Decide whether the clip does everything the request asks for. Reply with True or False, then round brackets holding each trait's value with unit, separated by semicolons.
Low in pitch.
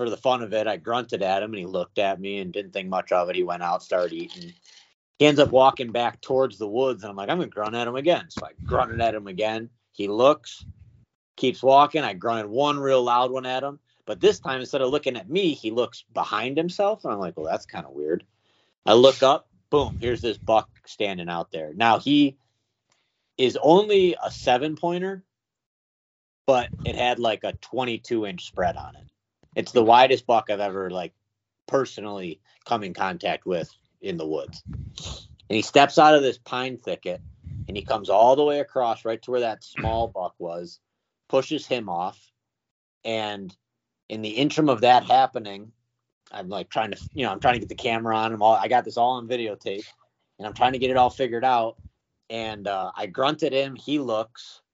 True (120 Hz)